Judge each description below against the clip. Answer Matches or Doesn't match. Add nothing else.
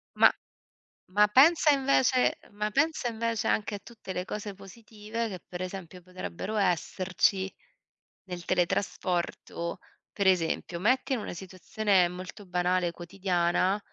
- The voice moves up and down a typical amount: Matches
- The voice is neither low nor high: Doesn't match